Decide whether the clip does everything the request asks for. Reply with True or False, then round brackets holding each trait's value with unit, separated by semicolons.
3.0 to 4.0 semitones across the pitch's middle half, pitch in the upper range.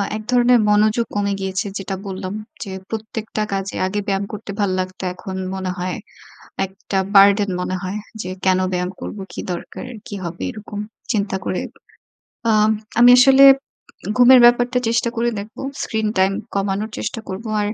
False (2.6 semitones; 205 Hz)